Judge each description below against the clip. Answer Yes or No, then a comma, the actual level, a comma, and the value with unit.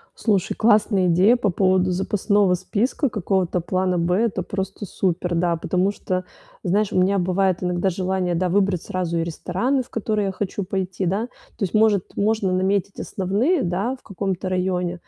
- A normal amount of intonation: No, narrow, 2.1 semitones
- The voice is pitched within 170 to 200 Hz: Yes, high, 190 Hz